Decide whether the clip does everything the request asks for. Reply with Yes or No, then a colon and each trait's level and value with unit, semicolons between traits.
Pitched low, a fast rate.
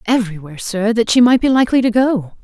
No: high, 225 Hz; fast, 220 wpm